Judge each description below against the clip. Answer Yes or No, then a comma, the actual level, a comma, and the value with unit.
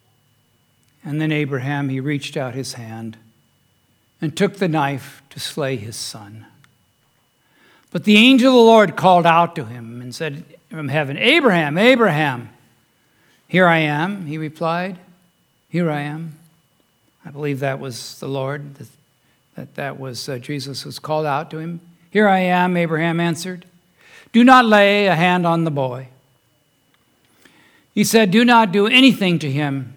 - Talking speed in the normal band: Yes, average, 155 wpm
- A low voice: No, medium, 150 Hz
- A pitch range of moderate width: Yes, average, 4.9 semitones